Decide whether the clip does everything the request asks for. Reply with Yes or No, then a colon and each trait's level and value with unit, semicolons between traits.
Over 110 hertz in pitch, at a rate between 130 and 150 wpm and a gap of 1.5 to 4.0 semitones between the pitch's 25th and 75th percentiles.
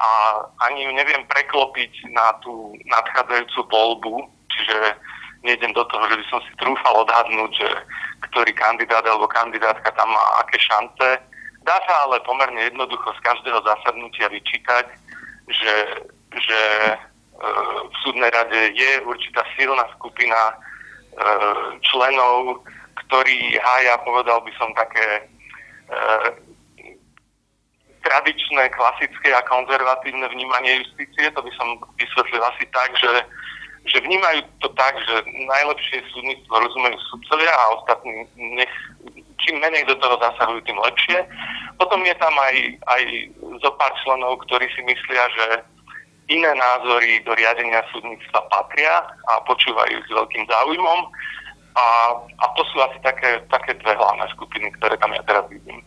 Yes: low, 120 Hz; average, 135 wpm; narrow, 2.4 semitones